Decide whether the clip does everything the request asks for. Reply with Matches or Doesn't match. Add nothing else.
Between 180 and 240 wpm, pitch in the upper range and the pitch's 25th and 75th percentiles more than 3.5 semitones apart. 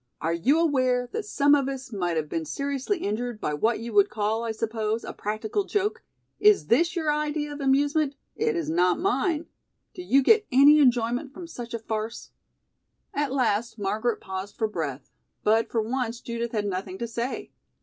Matches